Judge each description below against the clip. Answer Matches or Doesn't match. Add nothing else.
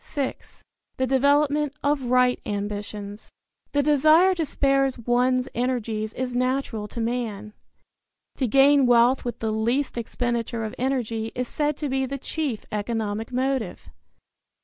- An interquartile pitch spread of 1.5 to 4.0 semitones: Matches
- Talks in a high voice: Matches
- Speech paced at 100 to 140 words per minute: Matches